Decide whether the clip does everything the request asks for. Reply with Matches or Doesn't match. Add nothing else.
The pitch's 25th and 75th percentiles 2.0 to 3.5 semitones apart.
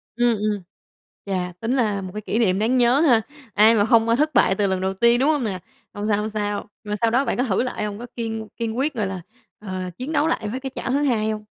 Matches